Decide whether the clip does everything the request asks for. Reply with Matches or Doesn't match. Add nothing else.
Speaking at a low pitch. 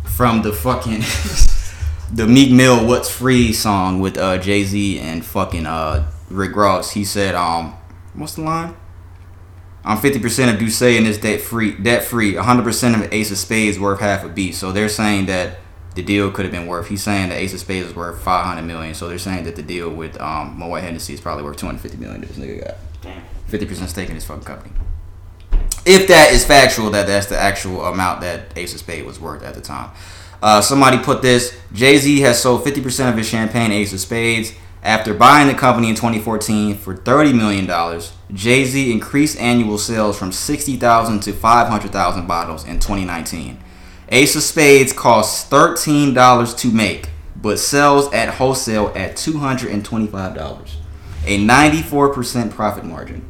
Matches